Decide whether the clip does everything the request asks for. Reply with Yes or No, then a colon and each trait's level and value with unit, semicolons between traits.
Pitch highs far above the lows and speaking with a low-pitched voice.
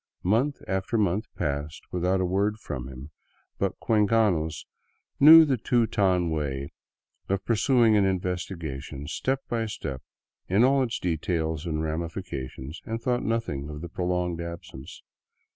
Yes: wide, 6.1 semitones; very low, 90 Hz